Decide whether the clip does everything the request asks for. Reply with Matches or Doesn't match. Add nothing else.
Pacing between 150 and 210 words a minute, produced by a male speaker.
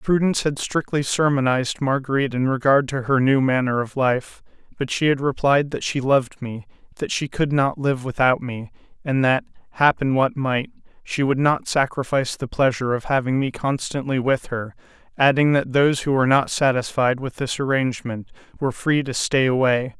Matches